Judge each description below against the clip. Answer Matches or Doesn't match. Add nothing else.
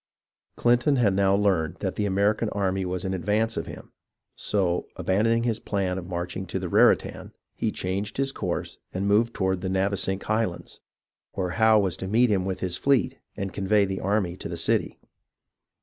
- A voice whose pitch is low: Matches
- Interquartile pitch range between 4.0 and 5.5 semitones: Doesn't match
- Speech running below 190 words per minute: Matches